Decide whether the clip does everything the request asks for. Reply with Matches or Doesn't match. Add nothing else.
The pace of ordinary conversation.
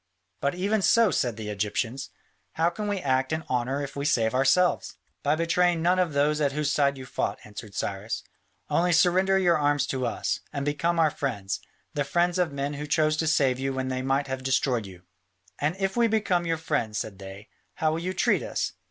Doesn't match